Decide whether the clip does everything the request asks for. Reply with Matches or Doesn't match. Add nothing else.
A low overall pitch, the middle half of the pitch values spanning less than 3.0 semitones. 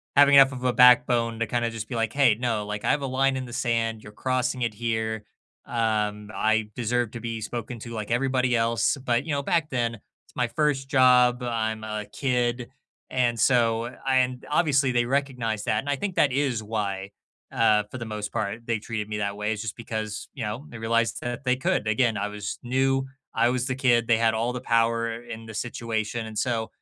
Matches